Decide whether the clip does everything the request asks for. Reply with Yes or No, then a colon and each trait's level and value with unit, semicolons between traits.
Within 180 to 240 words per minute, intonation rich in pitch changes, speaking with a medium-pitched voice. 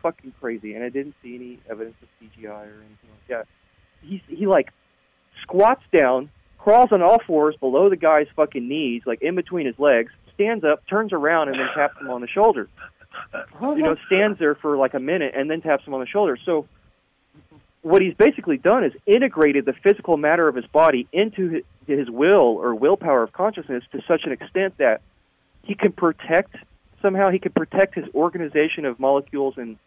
Yes: average, 195 wpm; wide, 6.7 semitones; medium, 150 Hz